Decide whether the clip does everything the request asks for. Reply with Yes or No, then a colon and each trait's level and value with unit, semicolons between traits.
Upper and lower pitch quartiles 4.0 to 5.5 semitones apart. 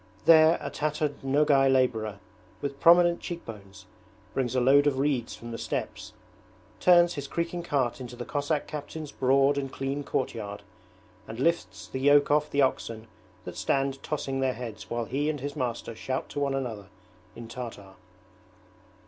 No: average, 3.4 semitones